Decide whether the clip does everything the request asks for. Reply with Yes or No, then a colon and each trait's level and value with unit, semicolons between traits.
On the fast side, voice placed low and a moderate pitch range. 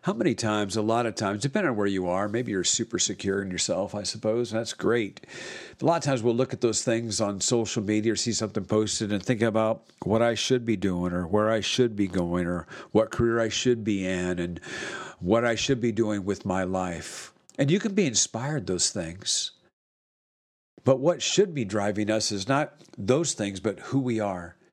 Yes: fast, 220 wpm; low, 110 Hz; average, 3.2 semitones